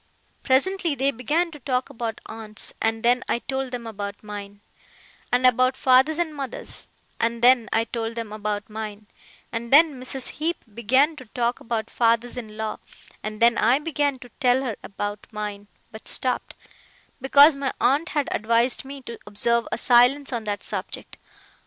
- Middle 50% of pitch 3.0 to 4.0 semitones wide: Yes, average, 3.4 semitones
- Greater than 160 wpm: Yes, average, 170 wpm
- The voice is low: No, high, 240 Hz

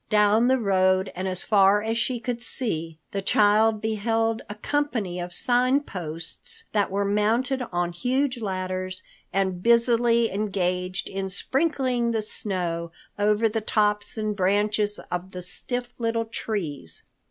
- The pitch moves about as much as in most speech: Yes, average, 3.8 semitones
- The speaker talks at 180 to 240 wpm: No, average, 140 wpm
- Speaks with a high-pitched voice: Yes, high, 210 Hz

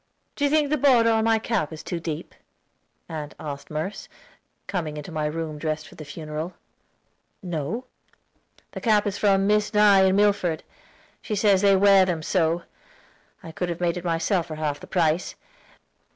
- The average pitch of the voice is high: No, medium, 175 Hz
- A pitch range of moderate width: Yes, average, 4.6 semitones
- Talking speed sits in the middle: Yes, average, 175 wpm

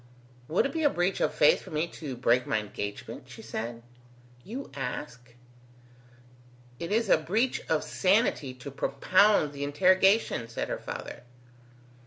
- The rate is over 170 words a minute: No, average, 150 wpm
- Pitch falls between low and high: Yes, medium, 150 Hz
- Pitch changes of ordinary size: No, wide, 7.4 semitones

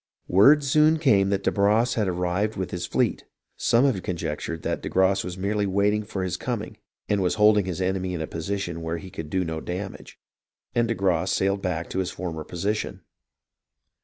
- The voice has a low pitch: Yes, very low, 95 Hz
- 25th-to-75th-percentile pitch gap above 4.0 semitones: No, average, 2.8 semitones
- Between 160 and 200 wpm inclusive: Yes, average, 195 wpm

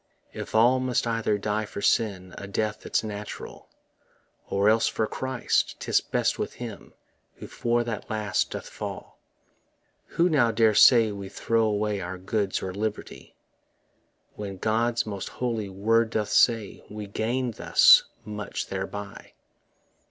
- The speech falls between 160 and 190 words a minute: No, average, 145 wpm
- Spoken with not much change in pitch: Yes, narrow, 2.3 semitones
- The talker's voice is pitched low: Yes, low, 110 Hz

